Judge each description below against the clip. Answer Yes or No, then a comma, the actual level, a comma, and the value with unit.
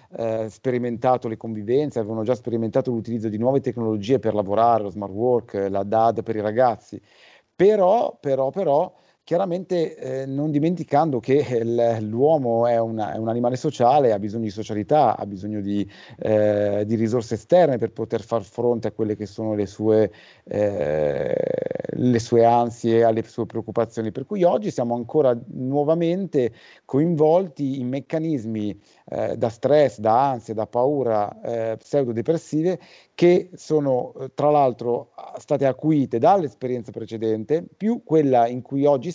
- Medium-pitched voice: No, low, 120 Hz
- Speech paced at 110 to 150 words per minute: Yes, average, 145 wpm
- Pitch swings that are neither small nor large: Yes, average, 4.6 semitones